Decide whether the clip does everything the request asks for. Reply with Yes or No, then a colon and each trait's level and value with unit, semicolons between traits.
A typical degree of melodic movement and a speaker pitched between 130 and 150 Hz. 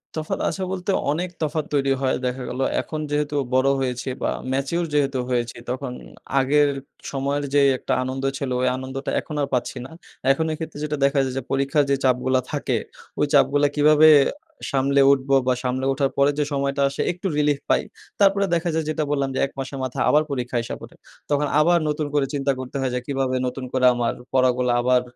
No: narrow, 2.3 semitones; medium, 140 Hz